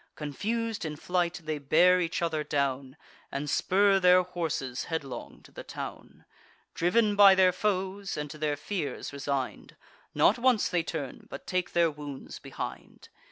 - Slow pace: No, average, 155 wpm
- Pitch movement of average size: Yes, average, 4.4 semitones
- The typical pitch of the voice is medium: Yes, medium, 170 Hz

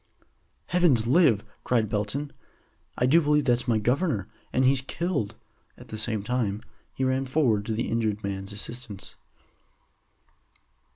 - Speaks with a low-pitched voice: Yes, low, 120 Hz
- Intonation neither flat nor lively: Yes, average, 4.2 semitones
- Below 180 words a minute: Yes, slow, 135 wpm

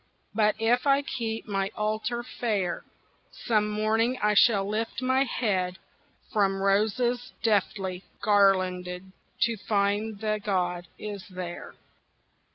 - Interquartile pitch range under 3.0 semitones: Yes, narrow, 2.6 semitones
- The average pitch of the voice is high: Yes, high, 210 Hz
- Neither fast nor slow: No, slow, 115 wpm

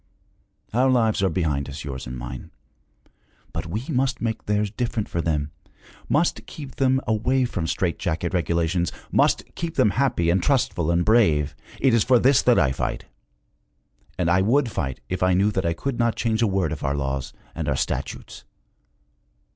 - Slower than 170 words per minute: No, average, 180 wpm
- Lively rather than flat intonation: Yes, wide, 6.8 semitones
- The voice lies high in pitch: No, very low, 95 Hz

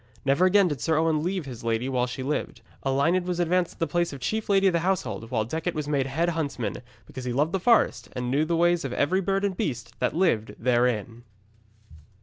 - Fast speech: Yes, fast, 225 wpm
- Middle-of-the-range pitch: Yes, medium, 155 Hz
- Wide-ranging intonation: Yes, wide, 5.8 semitones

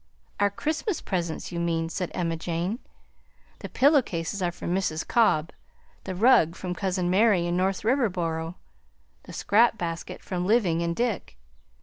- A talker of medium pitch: Yes, medium, 180 Hz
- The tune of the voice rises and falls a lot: No, average, 4.0 semitones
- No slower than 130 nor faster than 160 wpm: Yes, average, 150 wpm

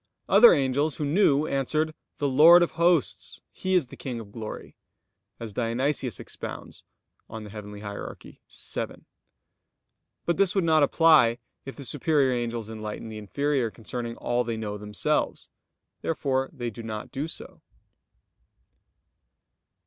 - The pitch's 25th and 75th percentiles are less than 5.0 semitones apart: No, wide, 5.4 semitones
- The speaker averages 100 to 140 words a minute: Yes, slow, 135 wpm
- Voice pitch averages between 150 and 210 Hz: No, low, 130 Hz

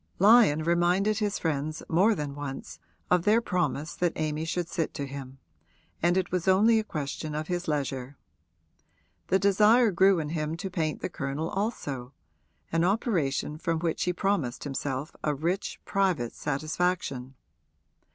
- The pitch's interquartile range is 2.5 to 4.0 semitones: No, average, 4.5 semitones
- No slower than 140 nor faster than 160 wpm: Yes, average, 150 wpm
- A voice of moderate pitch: Yes, medium, 165 Hz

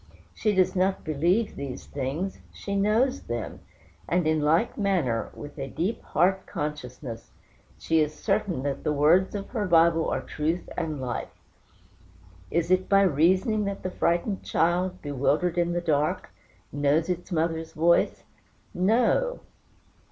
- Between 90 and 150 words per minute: Yes, average, 145 wpm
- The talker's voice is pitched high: No, medium, 170 Hz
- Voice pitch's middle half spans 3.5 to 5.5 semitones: Yes, average, 4.1 semitones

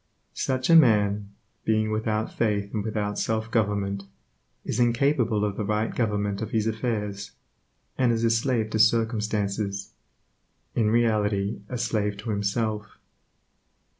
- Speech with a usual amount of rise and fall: No, narrow, 1.8 semitones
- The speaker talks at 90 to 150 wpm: Yes, slow, 135 wpm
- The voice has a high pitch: No, low, 110 Hz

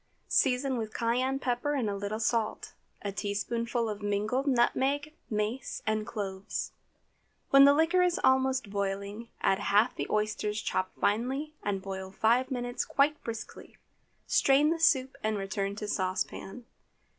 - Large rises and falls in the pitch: No, average, 4.4 semitones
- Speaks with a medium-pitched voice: No, high, 230 Hz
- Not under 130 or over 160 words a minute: Yes, average, 145 wpm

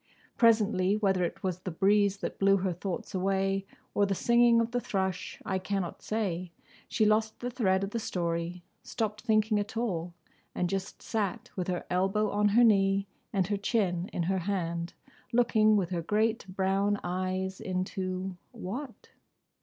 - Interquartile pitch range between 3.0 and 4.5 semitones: No, narrow, 2.6 semitones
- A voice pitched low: No, high, 195 Hz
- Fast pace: No, average, 155 wpm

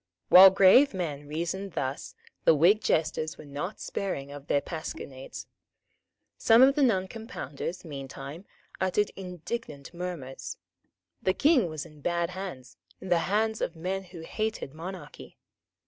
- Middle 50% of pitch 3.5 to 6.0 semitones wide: Yes, average, 4.7 semitones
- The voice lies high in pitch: No, medium, 175 Hz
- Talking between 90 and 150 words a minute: Yes, slow, 135 wpm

